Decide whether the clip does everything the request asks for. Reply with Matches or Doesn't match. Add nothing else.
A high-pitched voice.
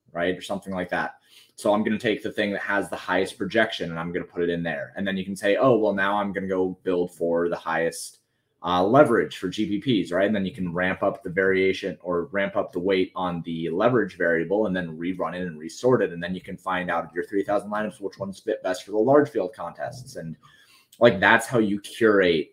Doesn't match